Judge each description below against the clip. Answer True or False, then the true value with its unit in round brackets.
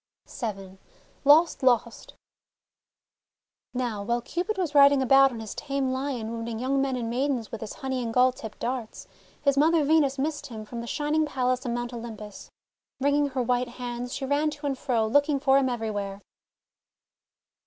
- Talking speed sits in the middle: True (170 wpm)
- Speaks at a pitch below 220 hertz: False (255 Hz)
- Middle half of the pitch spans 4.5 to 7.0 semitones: False (3.3 semitones)